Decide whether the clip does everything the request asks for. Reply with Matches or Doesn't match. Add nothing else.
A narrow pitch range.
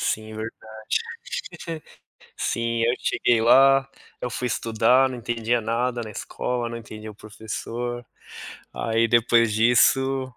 Matches